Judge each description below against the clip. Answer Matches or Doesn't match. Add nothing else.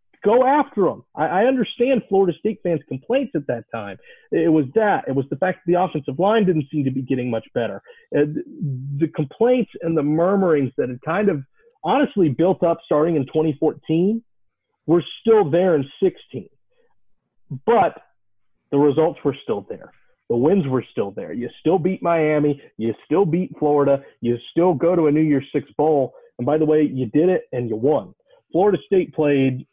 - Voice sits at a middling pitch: Matches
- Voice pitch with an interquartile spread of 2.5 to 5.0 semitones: Doesn't match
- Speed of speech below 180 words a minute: Doesn't match